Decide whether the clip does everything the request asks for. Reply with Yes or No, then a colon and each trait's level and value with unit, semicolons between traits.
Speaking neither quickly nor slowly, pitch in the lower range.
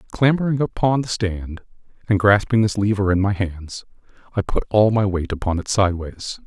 Yes: average, 175 wpm; low, 100 Hz